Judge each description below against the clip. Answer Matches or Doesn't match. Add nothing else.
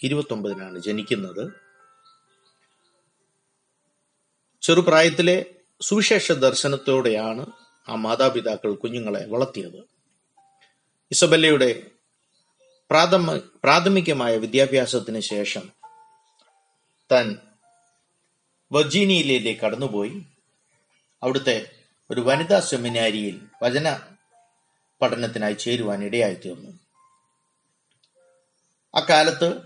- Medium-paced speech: Doesn't match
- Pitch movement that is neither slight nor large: Doesn't match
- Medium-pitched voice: Matches